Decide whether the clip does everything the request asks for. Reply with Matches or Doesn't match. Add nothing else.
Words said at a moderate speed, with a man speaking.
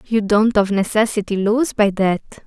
Doesn't match